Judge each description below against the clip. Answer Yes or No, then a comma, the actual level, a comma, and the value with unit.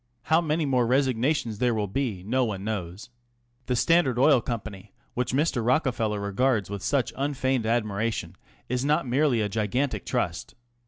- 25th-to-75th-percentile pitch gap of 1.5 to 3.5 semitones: No, average, 4.0 semitones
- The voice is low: Yes, low, 120 Hz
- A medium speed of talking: Yes, average, 155 wpm